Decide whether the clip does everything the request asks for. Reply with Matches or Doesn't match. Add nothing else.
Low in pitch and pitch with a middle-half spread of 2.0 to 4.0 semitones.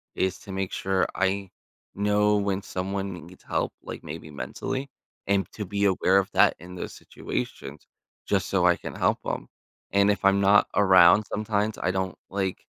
Doesn't match